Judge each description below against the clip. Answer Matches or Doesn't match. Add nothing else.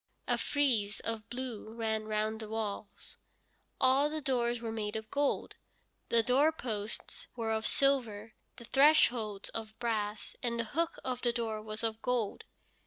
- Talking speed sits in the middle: Matches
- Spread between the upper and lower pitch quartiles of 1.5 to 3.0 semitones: Matches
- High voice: Matches